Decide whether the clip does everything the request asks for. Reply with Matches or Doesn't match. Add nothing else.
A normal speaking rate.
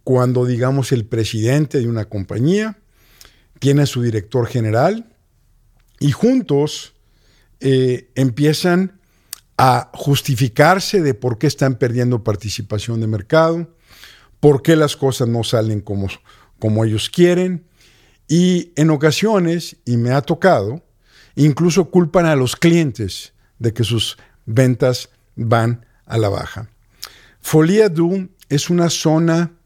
Doesn't match